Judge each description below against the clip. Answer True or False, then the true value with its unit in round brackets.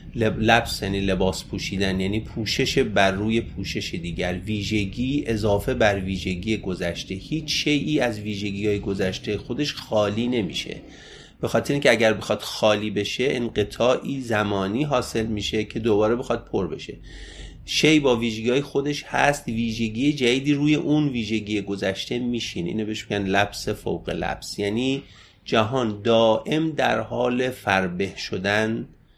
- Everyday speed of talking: True (140 wpm)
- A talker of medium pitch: False (110 Hz)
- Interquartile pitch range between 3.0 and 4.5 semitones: True (3.9 semitones)